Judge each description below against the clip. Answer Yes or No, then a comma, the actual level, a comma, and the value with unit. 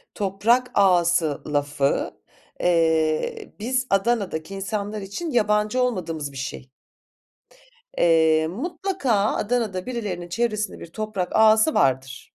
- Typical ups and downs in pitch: No, wide, 6.3 semitones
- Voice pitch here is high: Yes, high, 195 Hz